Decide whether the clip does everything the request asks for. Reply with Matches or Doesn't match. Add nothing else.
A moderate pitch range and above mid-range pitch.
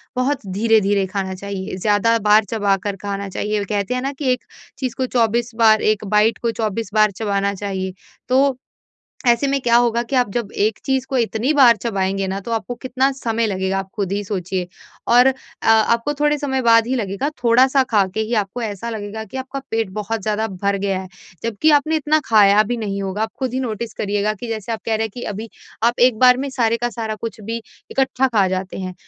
Matches